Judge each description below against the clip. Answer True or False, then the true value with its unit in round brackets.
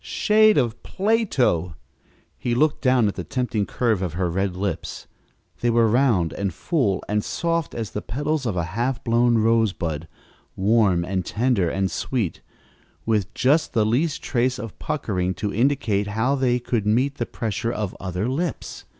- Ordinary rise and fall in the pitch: True (4.9 semitones)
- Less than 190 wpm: True (165 wpm)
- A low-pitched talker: True (115 Hz)